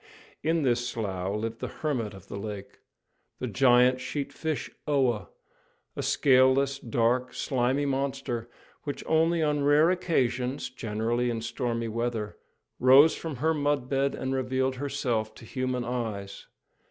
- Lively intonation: No, average, 3.2 semitones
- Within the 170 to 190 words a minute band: No, slow, 135 wpm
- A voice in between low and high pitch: No, low, 125 Hz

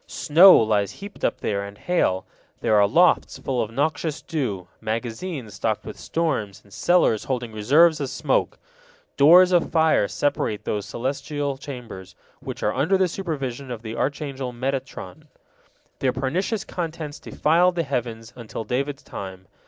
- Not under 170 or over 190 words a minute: No, average, 150 wpm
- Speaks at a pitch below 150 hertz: Yes, low, 135 Hz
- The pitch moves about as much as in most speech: No, wide, 6.3 semitones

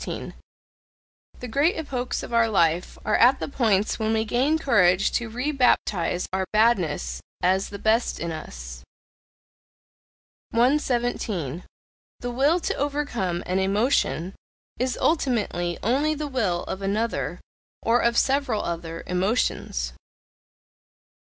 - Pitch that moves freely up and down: Yes, wide, 5.9 semitones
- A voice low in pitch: No, high, 220 Hz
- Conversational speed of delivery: No, slow, 120 wpm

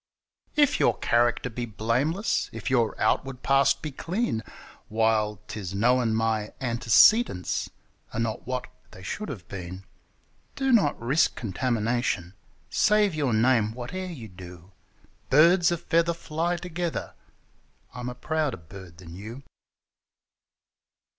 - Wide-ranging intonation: Yes, wide, 6.5 semitones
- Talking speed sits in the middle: No, slow, 125 wpm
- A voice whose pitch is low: Yes, low, 120 Hz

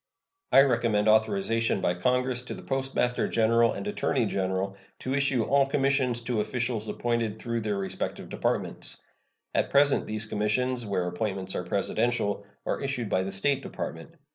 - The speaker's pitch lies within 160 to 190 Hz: No, low, 115 Hz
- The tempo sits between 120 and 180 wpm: Yes, average, 155 wpm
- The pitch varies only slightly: No, average, 3.9 semitones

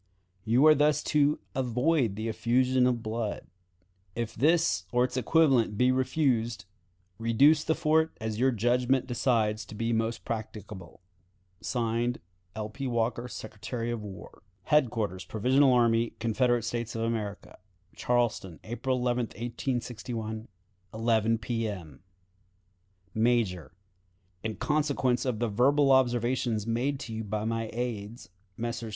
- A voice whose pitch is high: No, low, 120 Hz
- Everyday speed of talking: No, slow, 125 wpm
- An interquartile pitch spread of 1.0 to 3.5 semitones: Yes, narrow, 2.5 semitones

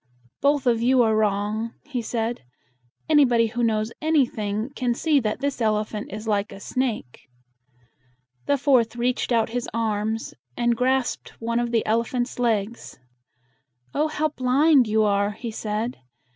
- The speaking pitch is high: Yes, high, 235 Hz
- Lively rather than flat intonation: No, average, 2.8 semitones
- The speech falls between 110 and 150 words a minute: Yes, average, 145 wpm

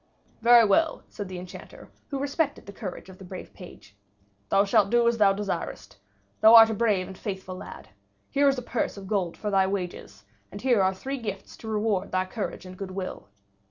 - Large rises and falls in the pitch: No, average, 3.6 semitones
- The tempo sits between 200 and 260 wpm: Yes, fast, 205 wpm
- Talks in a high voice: Yes, high, 200 Hz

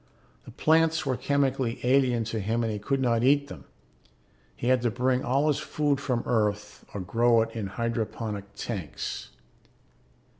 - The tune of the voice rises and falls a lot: No, average, 3.4 semitones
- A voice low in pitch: Yes, low, 120 Hz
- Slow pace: No, average, 160 wpm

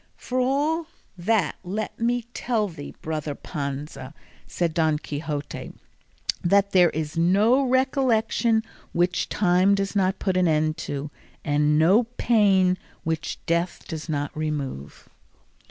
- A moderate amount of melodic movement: No, wide, 5.9 semitones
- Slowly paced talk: Yes, slow, 125 wpm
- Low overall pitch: No, medium, 180 Hz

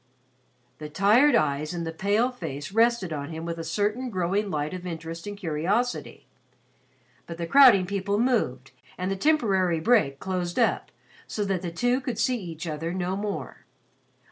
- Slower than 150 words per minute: No, average, 170 wpm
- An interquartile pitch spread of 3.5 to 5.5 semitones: Yes, average, 4.6 semitones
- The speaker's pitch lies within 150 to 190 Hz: Yes, medium, 185 Hz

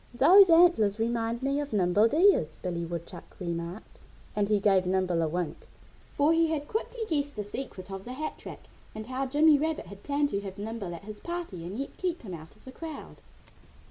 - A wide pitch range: Yes, wide, 7.7 semitones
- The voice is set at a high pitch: Yes, high, 220 Hz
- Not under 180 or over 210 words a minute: Yes, fast, 205 wpm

